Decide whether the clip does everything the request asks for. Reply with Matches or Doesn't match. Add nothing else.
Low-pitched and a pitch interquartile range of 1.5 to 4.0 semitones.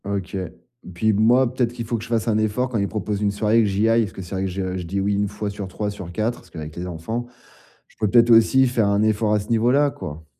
Matches